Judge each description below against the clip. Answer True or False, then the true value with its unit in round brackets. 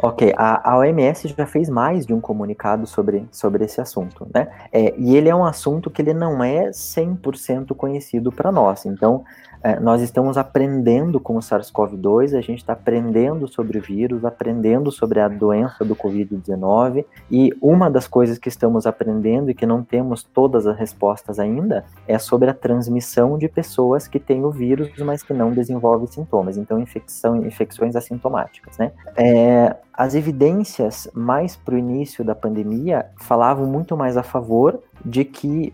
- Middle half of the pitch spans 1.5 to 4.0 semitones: True (3.3 semitones)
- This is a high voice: False (120 Hz)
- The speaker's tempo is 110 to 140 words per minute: False (170 wpm)